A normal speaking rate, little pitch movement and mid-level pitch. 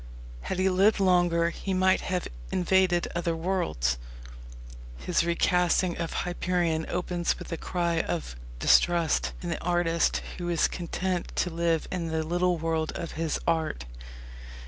Yes: average, 145 wpm; narrow, 1.6 semitones; medium, 170 Hz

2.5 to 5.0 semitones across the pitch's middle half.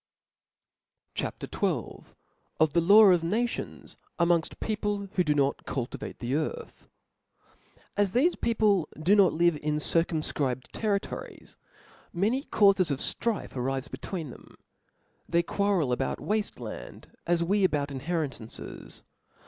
No: wide, 5.4 semitones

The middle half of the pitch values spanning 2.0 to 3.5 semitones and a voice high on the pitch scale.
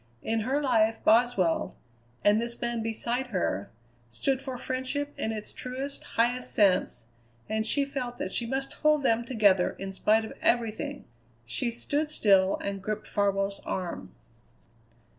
No: average, 4.2 semitones; high, 230 Hz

